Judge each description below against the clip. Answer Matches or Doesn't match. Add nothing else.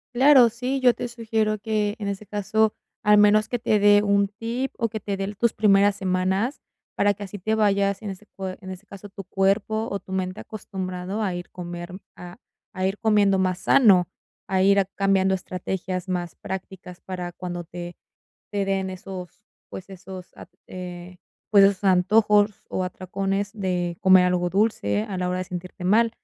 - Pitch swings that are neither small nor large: Doesn't match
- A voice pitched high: Matches